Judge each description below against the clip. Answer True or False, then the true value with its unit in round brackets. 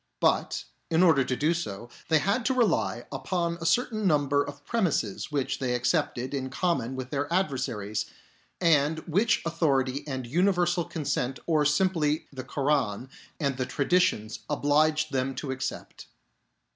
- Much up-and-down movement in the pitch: False (4.4 semitones)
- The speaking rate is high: False (150 wpm)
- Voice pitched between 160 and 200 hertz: False (145 Hz)